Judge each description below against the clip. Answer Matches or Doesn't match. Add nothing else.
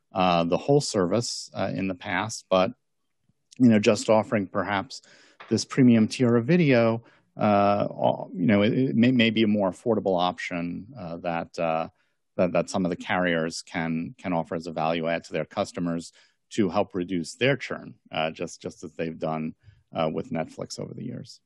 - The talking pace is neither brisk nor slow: Matches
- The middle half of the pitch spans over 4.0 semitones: Matches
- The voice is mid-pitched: Doesn't match